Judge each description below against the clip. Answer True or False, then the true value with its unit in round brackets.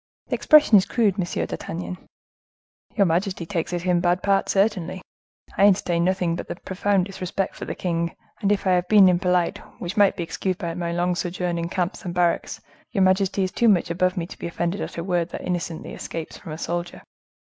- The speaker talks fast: True (210 wpm)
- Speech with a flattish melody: True (2.1 semitones)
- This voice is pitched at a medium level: True (180 Hz)